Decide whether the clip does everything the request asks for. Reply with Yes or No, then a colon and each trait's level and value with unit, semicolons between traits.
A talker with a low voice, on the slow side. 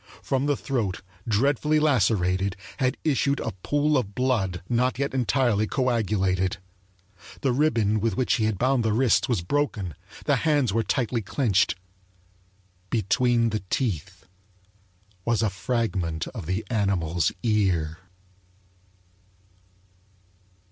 Yes: low, 115 Hz; slow, 120 wpm